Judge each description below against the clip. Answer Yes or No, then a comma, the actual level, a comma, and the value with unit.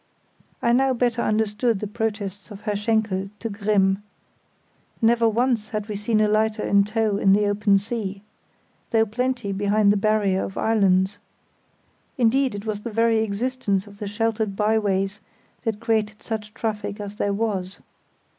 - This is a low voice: No, high, 210 Hz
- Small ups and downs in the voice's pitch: Yes, narrow, 1.9 semitones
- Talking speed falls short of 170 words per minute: Yes, average, 155 wpm